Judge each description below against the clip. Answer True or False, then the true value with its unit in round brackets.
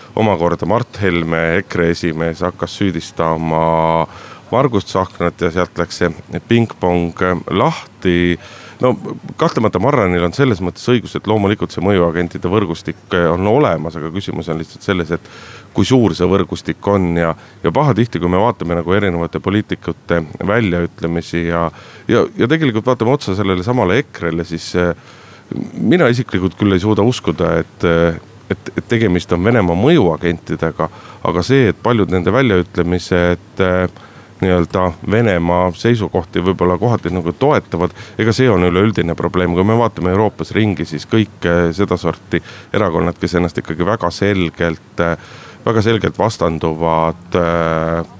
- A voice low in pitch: True (90 Hz)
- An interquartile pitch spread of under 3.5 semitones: False (3.8 semitones)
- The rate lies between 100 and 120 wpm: False (135 wpm)